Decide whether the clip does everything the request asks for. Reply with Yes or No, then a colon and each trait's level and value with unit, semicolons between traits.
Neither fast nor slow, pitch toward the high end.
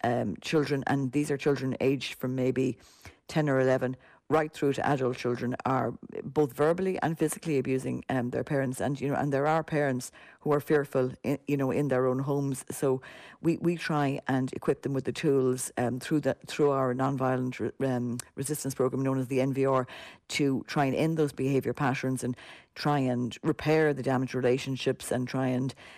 No: average, 195 wpm; low, 135 Hz